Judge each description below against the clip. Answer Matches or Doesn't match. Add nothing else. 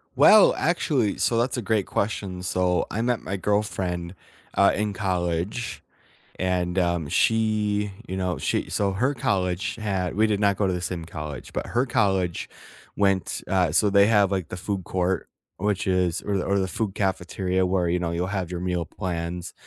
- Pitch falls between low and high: Doesn't match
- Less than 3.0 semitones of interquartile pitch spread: Matches